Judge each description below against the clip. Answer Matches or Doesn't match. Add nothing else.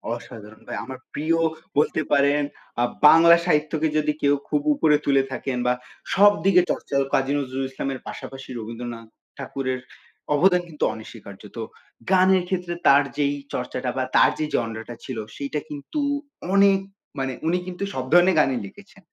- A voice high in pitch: Doesn't match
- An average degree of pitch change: Matches